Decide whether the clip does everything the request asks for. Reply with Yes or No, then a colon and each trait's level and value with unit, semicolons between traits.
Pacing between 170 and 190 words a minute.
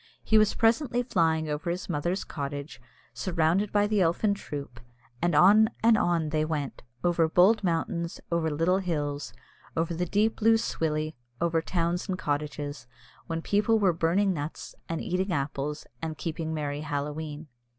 No: average, 155 wpm